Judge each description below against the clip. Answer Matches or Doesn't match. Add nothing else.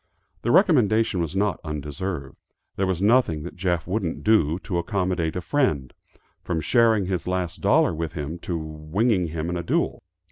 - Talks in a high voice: Doesn't match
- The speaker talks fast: Doesn't match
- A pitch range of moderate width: Matches